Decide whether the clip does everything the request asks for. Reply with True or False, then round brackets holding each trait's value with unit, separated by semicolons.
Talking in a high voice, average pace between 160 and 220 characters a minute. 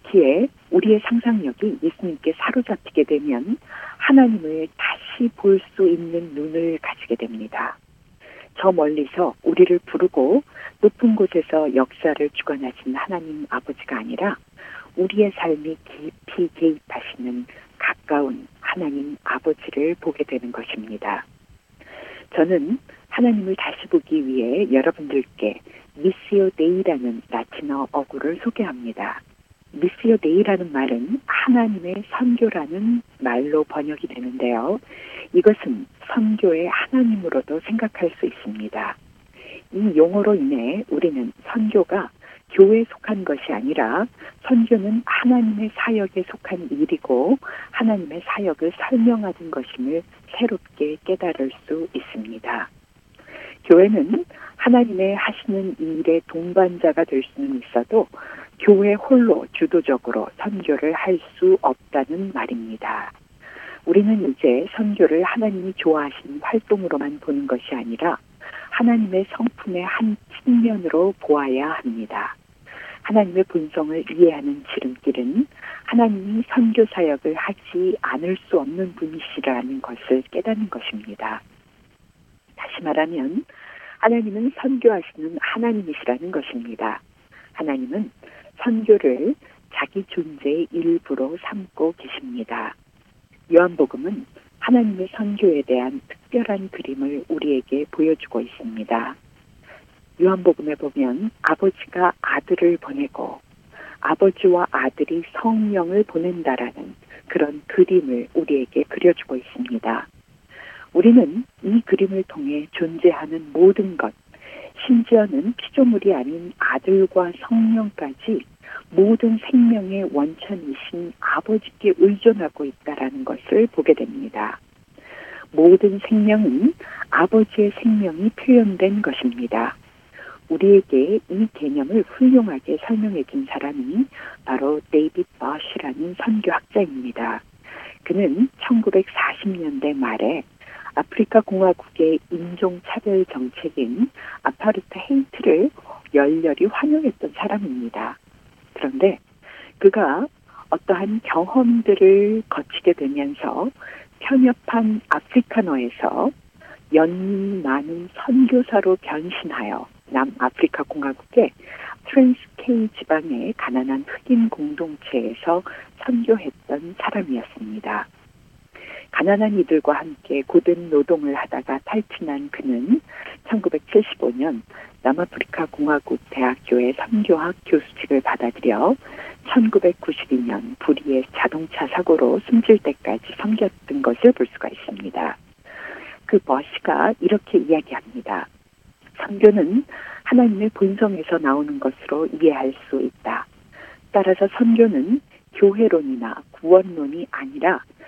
False (195 Hz; 260 characters per minute)